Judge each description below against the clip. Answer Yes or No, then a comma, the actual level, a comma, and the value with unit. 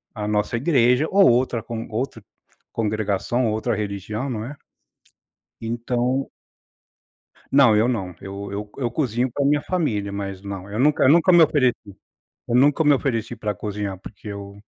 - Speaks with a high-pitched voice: No, low, 115 Hz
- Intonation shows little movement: No, average, 4.2 semitones